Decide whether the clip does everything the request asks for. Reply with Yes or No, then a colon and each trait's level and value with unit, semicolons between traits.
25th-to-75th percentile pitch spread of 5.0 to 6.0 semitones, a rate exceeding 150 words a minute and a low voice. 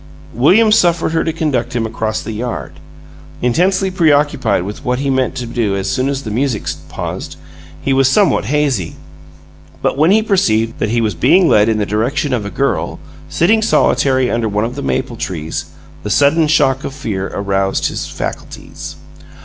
Yes: wide, 5.5 semitones; average, 180 wpm; low, 130 Hz